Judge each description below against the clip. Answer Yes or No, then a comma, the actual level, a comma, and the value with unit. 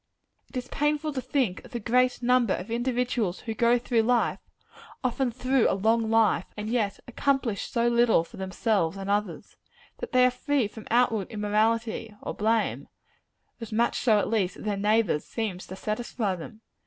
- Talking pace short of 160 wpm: No, average, 180 wpm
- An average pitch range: Yes, average, 3.0 semitones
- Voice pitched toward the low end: No, high, 225 Hz